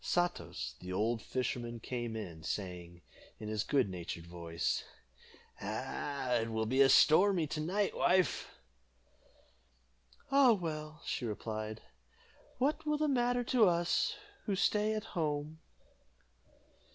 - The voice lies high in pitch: No, medium, 140 Hz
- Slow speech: Yes, slow, 115 wpm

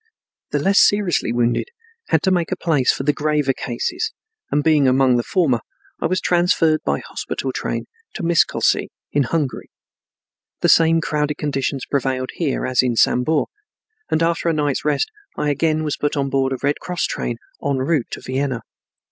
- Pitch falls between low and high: Yes, medium, 145 Hz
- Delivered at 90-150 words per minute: No, average, 175 wpm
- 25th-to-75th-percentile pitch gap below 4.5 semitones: Yes, average, 3.7 semitones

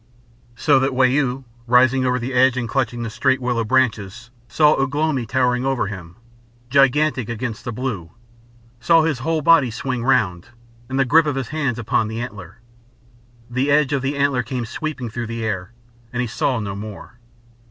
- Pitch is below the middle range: Yes, low, 125 Hz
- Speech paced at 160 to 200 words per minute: Yes, average, 180 wpm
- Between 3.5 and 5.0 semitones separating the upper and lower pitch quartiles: No, average, 2.8 semitones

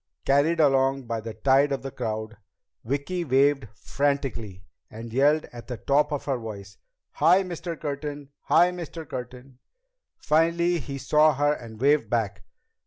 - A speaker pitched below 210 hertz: Yes, medium, 140 Hz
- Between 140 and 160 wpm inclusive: Yes, average, 150 wpm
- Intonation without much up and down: No, average, 4.1 semitones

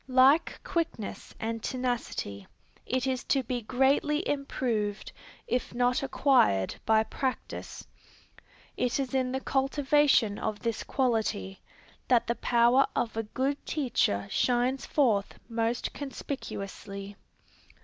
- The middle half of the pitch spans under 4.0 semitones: Yes, average, 3.3 semitones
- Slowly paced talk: Yes, slow, 115 wpm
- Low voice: No, very high, 250 Hz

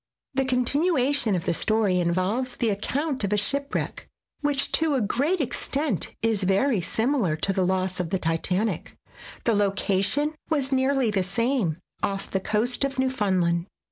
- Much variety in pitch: Yes, wide, 6.0 semitones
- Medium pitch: No, high, 220 Hz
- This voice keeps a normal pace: Yes, average, 170 wpm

